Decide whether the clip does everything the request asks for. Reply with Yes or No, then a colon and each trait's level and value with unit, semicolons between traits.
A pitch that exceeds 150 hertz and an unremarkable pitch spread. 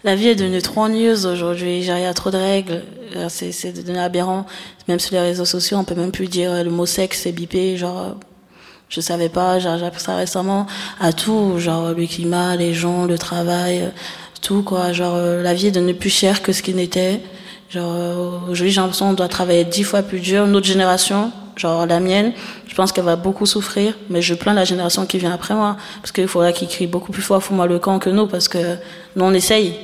No: medium, 185 Hz; narrow, 1.9 semitones